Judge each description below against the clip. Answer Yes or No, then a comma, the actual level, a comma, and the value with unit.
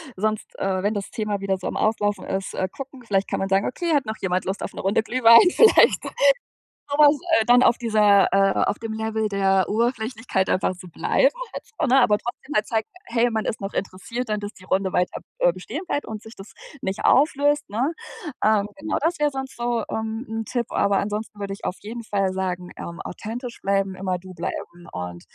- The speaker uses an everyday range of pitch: Yes, average, 3.7 semitones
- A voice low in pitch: No, high, 215 Hz